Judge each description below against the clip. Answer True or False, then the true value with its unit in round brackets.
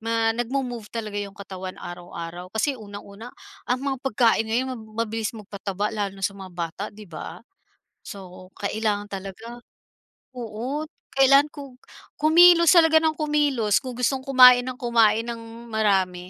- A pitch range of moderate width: True (4.2 semitones)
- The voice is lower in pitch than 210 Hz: False (225 Hz)